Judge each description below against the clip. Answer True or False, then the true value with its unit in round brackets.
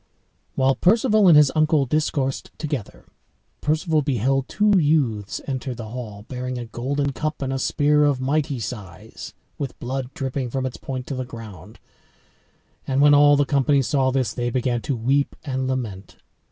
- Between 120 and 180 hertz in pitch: True (135 Hz)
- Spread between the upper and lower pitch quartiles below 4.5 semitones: True (2.8 semitones)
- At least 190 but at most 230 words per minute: False (165 wpm)